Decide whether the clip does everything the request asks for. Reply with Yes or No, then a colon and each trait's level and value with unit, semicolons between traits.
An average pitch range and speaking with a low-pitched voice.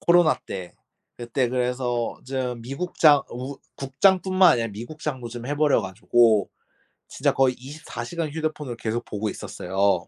Yes: average, 4.4 semitones; low, 125 Hz